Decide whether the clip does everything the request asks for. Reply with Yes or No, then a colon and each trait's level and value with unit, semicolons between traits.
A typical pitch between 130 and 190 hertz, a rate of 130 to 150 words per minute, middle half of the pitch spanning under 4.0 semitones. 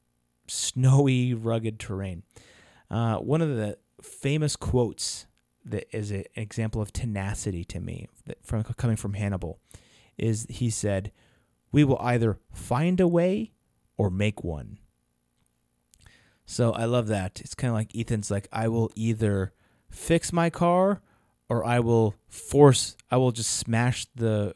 No: low, 110 Hz; average, 145 wpm; average, 3.5 semitones